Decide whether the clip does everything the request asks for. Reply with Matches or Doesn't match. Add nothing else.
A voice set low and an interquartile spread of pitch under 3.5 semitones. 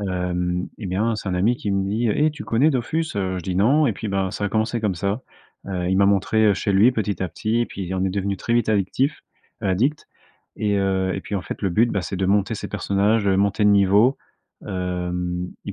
Matches